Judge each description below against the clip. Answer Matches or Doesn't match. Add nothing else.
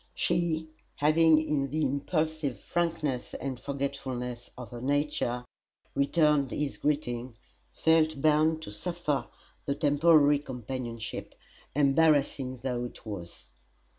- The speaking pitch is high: Doesn't match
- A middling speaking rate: Doesn't match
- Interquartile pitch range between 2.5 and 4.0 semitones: Matches